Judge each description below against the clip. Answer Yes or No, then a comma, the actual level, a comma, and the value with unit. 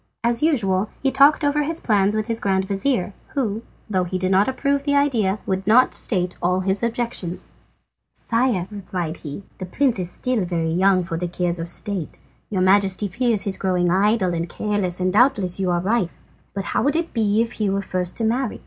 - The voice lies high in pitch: Yes, high, 200 Hz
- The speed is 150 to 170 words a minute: No, fast, 205 wpm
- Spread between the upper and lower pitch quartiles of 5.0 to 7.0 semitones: No, average, 4.3 semitones